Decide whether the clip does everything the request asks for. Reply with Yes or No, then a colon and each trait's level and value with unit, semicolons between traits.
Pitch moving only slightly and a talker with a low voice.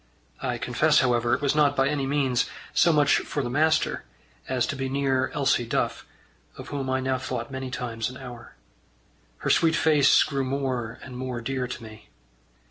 Yes: narrow, 2.3 semitones; low, 130 Hz